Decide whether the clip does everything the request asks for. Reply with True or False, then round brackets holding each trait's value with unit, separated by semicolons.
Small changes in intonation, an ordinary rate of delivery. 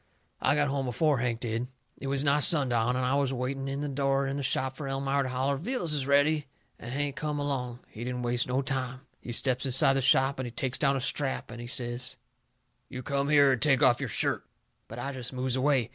False (1.9 semitones; 235 wpm)